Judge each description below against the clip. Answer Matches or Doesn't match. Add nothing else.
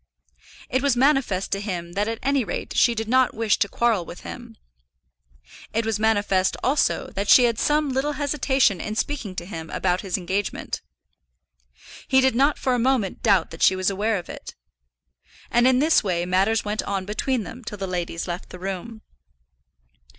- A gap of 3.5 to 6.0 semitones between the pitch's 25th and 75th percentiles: Matches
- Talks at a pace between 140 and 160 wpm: Doesn't match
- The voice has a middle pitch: Doesn't match